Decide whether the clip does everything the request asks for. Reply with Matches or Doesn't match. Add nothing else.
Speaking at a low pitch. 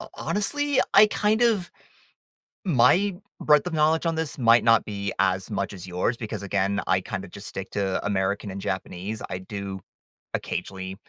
Matches